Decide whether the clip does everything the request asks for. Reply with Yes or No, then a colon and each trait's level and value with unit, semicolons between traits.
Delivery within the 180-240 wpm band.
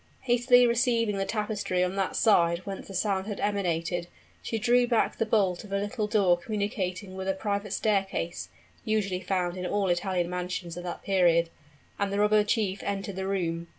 Yes: average, 185 wpm